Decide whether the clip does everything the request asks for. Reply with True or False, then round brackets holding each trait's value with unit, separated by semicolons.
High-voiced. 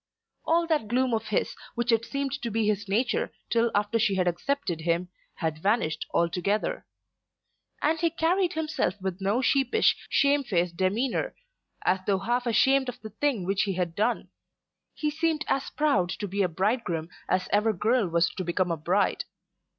True (215 Hz)